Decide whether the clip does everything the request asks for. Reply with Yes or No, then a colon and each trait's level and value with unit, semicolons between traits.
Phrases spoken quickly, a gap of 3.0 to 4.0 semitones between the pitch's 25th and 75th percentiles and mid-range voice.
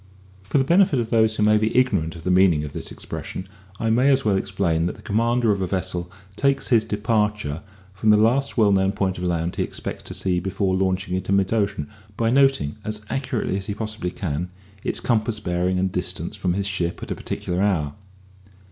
No: fast, 210 wpm; average, 3.5 semitones; low, 100 Hz